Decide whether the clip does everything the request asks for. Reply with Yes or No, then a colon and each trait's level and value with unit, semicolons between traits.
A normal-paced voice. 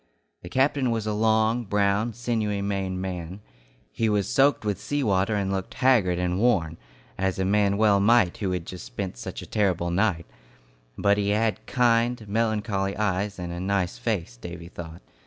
Yes: average, 175 wpm